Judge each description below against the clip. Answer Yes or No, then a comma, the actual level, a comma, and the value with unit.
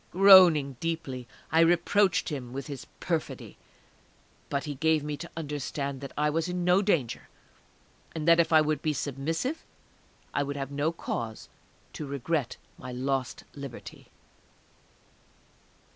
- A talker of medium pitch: Yes, medium, 150 Hz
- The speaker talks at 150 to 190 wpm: No, average, 140 wpm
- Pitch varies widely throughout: No, average, 3.2 semitones